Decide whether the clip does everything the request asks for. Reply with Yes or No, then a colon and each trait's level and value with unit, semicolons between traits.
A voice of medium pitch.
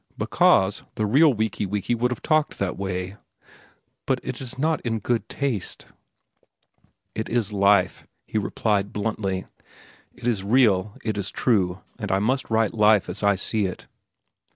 No: low, 105 Hz